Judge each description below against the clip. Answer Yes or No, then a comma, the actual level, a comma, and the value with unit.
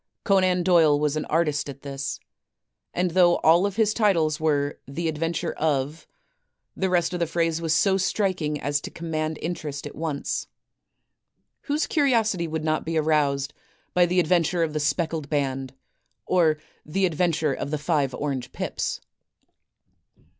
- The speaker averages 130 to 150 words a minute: No, average, 160 wpm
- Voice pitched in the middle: Yes, medium, 160 Hz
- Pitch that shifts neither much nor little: Yes, average, 3.2 semitones